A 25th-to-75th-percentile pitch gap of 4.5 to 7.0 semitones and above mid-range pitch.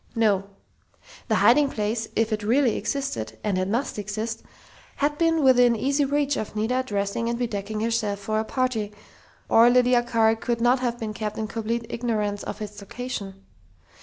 No: average, 2.9 semitones; high, 225 Hz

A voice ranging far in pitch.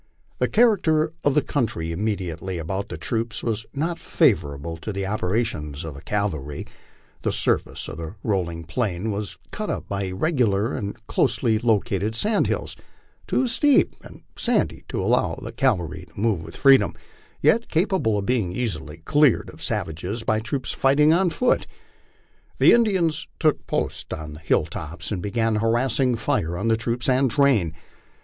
Yes: wide, 7.3 semitones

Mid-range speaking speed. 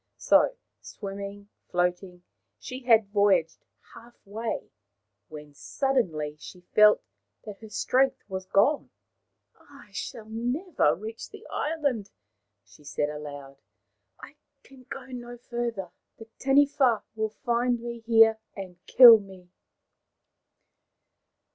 No: slow, 115 wpm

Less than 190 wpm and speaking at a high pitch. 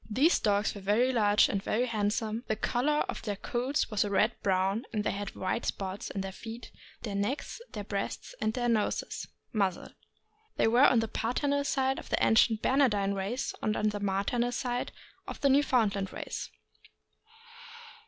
Yes: average, 180 wpm; high, 220 Hz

